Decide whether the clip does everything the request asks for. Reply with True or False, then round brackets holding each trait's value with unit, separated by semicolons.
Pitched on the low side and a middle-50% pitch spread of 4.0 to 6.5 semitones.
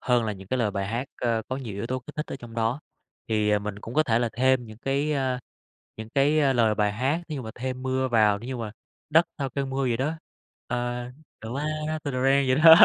False (125 Hz; 3.4 semitones)